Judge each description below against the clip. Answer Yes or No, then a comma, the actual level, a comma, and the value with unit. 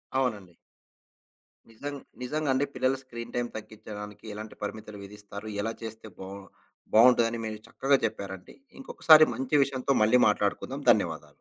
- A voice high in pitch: No, low, 110 Hz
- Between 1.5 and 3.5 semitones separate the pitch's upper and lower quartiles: No, average, 3.9 semitones